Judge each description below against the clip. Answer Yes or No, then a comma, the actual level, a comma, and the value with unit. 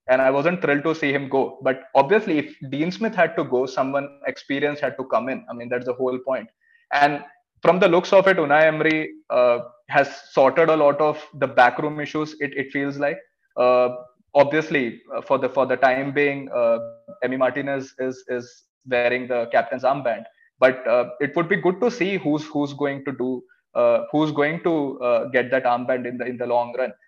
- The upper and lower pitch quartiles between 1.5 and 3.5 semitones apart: No, average, 4.4 semitones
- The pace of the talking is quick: Yes, fast, 210 wpm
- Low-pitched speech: No, medium, 145 Hz